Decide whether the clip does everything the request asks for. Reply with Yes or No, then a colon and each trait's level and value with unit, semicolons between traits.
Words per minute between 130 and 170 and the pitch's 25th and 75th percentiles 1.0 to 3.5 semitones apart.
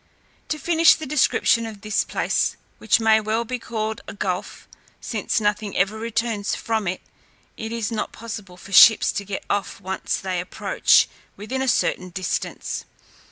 Yes: average, 165 wpm; narrow, 2.6 semitones